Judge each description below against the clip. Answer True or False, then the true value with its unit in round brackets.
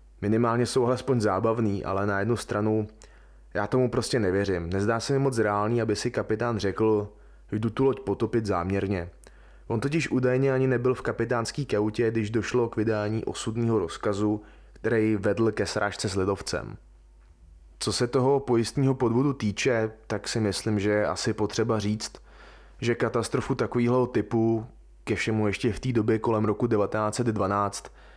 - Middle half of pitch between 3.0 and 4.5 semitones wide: False (2.6 semitones)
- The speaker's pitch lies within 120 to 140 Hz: False (110 Hz)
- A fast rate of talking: False (155 wpm)